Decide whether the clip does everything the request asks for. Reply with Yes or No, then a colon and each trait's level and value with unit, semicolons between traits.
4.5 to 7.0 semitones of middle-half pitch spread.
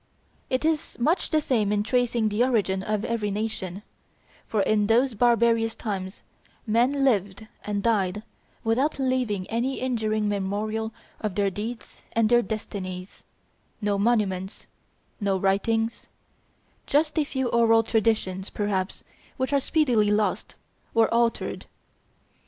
No: average, 2.8 semitones